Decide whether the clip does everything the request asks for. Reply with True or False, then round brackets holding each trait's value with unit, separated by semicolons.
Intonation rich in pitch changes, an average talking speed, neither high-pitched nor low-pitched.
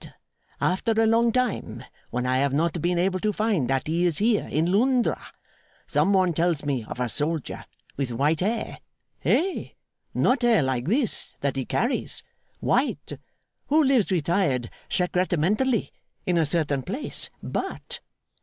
True (7.6 semitones; 150 wpm; 175 Hz)